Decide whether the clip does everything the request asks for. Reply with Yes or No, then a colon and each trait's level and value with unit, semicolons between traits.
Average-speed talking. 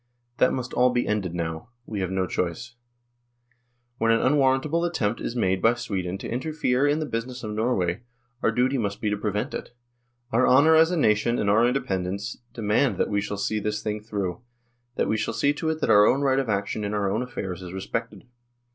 No: fast, 210 wpm